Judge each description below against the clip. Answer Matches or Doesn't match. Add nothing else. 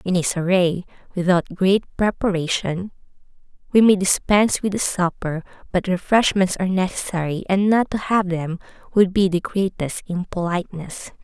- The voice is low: Doesn't match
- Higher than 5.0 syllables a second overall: Doesn't match